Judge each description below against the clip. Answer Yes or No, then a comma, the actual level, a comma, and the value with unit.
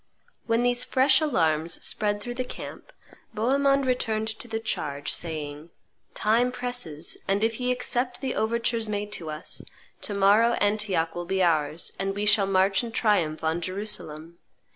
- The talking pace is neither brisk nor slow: Yes, average, 160 wpm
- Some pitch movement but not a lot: No, wide, 5.9 semitones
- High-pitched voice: Yes, high, 210 Hz